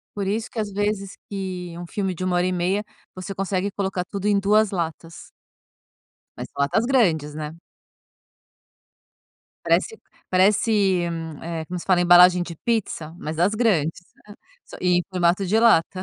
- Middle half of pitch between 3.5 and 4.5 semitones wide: No, average, 2.8 semitones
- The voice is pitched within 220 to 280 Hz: No, medium, 185 Hz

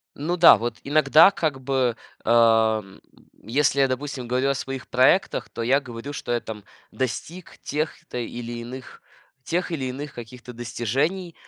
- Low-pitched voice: Yes, low, 130 Hz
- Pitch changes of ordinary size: Yes, average, 3.6 semitones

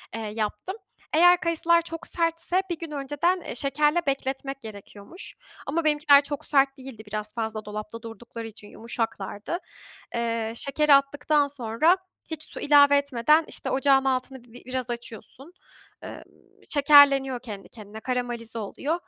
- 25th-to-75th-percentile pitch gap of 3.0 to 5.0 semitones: Yes, average, 4.7 semitones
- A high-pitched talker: Yes, very high, 270 Hz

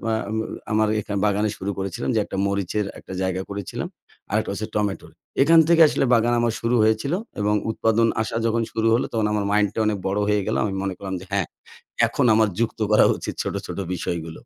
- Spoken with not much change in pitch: Yes, narrow, 2.3 semitones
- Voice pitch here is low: Yes, low, 105 Hz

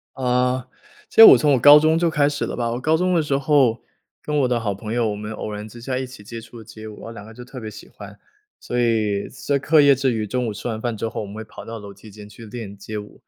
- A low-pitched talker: Yes, low, 115 Hz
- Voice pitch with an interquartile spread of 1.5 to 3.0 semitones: No, average, 3.7 semitones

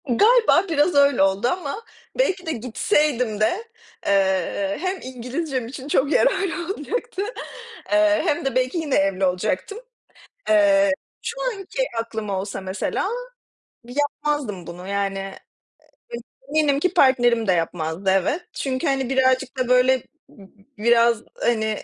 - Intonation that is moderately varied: No, wide, 6.8 semitones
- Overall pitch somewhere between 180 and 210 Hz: No, very high, 260 Hz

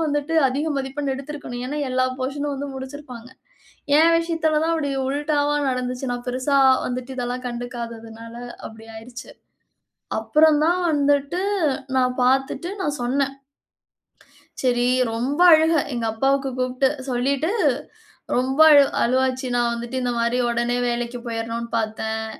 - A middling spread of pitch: Yes, average, 3.1 semitones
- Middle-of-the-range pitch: No, very high, 260 Hz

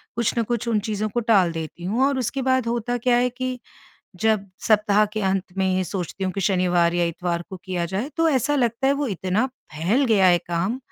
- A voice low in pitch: No, high, 210 Hz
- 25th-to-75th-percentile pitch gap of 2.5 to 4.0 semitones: No, average, 4.8 semitones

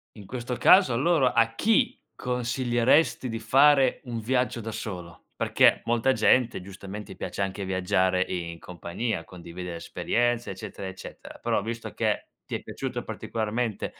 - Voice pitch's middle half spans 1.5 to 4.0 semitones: No, average, 4.7 semitones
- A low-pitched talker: Yes, low, 115 Hz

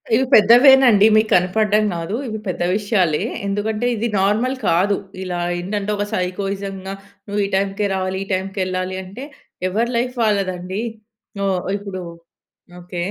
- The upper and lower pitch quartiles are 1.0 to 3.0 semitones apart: Yes, narrow, 2.5 semitones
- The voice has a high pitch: Yes, high, 200 Hz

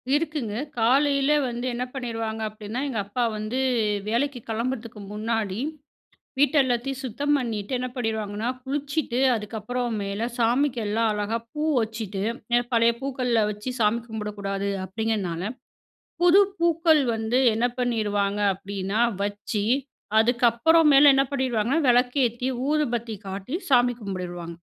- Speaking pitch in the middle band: No, high, 230 Hz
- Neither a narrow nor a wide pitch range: Yes, average, 3.8 semitones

